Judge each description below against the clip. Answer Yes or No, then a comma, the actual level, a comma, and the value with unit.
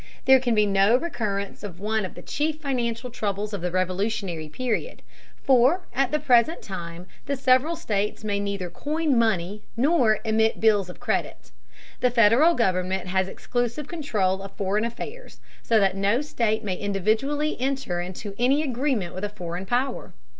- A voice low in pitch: No, high, 220 Hz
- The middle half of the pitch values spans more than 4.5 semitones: Yes, average, 5.0 semitones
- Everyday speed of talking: Yes, average, 165 wpm